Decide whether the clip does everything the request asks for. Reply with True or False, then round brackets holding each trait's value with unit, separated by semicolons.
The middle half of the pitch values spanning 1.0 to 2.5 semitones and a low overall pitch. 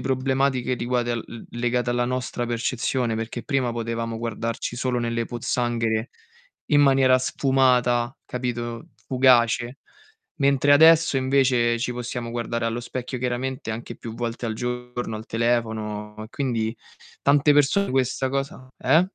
True (2.0 semitones; 120 Hz)